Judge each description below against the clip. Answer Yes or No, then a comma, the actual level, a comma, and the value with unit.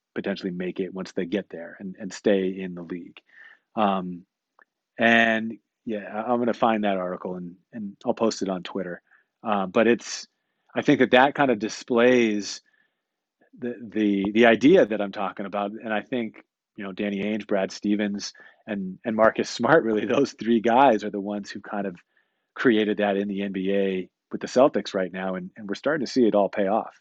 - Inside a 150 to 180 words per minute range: No, average, 200 wpm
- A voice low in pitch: Yes, low, 105 Hz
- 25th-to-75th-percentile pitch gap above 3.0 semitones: No, average, 2.7 semitones